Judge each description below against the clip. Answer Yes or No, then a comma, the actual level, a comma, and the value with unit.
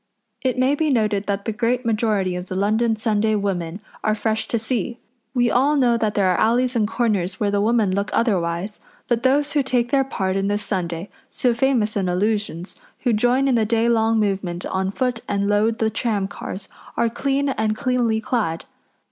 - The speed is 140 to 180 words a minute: No, average, 195 wpm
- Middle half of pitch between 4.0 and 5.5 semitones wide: No, average, 3.2 semitones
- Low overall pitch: No, high, 220 Hz